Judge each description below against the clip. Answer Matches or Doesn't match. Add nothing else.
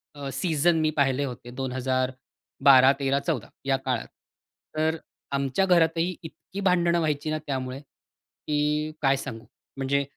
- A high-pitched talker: Doesn't match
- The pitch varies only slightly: Doesn't match